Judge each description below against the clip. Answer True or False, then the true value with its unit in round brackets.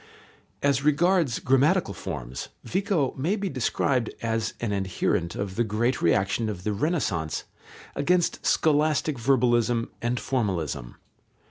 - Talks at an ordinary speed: False (120 wpm)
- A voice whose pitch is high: False (120 Hz)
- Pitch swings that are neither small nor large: False (6.8 semitones)